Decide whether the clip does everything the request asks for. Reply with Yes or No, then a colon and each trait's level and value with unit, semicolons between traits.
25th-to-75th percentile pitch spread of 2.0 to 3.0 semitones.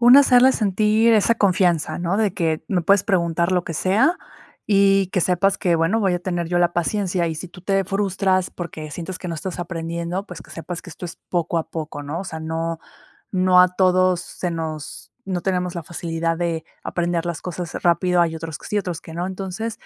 Yes: narrow, 2.5 semitones